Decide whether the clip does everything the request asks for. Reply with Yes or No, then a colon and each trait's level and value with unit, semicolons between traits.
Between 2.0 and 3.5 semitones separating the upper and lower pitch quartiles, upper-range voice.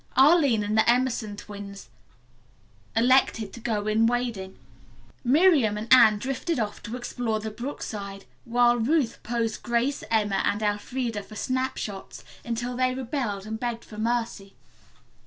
Yes: average, 3.0 semitones; high, 230 Hz